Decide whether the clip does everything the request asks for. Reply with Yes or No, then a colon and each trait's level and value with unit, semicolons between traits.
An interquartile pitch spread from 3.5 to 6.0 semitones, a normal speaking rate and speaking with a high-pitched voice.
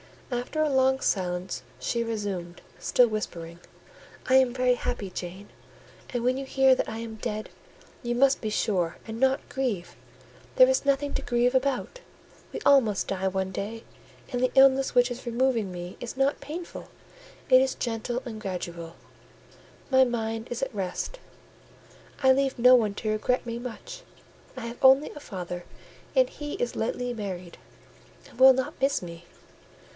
Yes: average, 4.4 semitones; average, 165 wpm; high, 240 Hz